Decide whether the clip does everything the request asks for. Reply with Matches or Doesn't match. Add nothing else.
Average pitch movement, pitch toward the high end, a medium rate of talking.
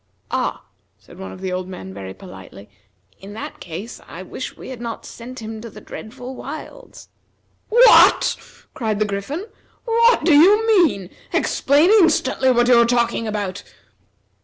Doesn't match